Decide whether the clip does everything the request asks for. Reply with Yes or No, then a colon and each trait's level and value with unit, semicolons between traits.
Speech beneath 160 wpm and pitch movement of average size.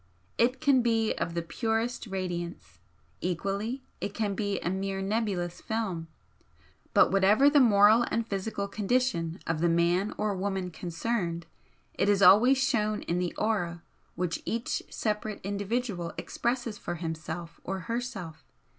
Yes: average, 140 wpm; average, 4.5 semitones